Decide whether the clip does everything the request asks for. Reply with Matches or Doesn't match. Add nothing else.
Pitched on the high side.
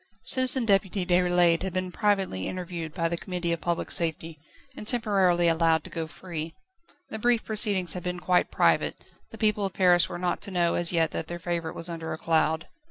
Doesn't match